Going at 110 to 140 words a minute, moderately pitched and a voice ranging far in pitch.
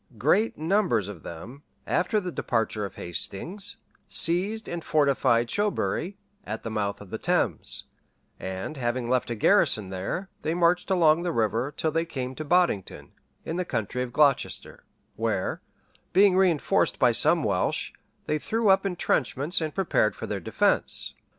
No: average, 155 wpm; medium, 150 Hz; wide, 7.9 semitones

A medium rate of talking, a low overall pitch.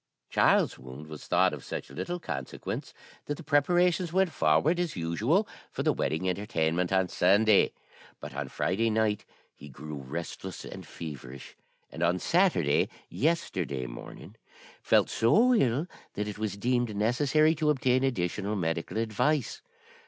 Yes: average, 145 wpm; low, 105 Hz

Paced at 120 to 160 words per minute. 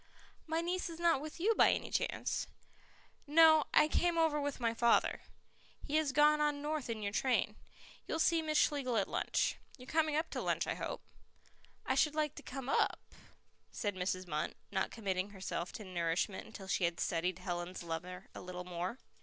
No: average, 185 wpm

